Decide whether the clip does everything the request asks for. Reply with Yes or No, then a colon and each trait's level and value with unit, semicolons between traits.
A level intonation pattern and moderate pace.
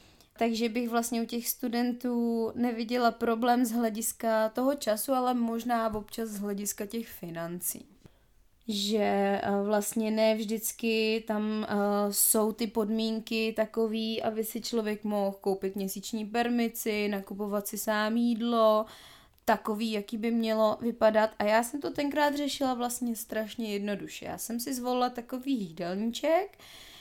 Yes: narrow, 1.8 semitones; average, 130 wpm